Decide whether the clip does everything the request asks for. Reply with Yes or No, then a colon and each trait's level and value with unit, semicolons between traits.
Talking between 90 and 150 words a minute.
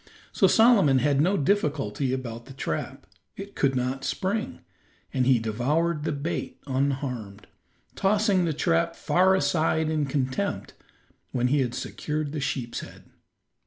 Yes: average, 140 wpm